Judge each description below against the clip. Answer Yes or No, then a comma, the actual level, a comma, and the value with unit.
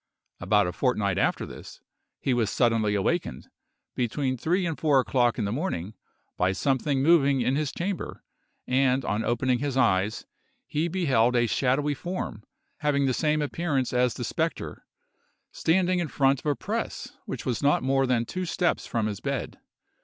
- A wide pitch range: No, average, 4.2 semitones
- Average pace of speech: Yes, average, 170 wpm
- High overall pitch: No, low, 130 Hz